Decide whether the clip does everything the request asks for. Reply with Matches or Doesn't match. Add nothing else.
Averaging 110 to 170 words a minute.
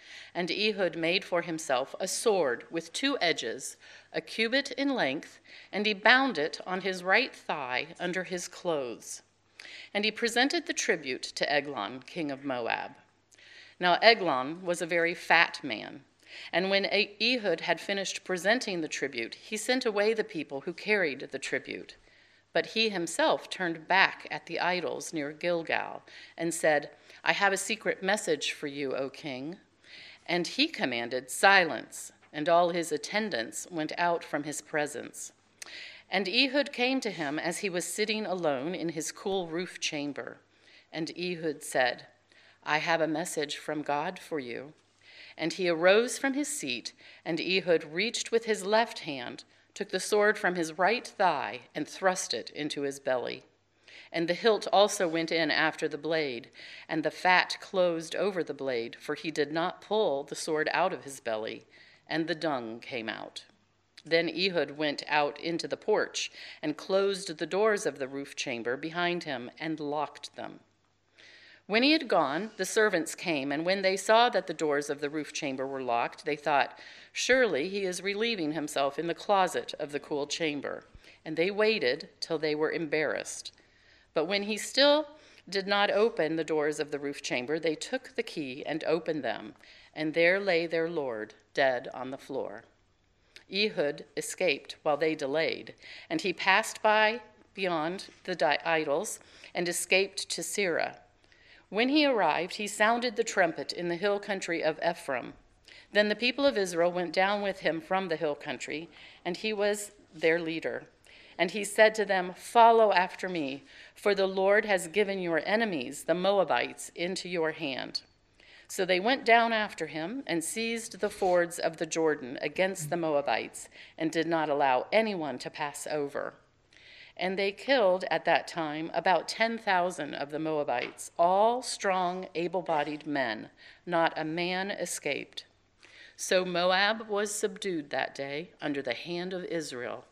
Matches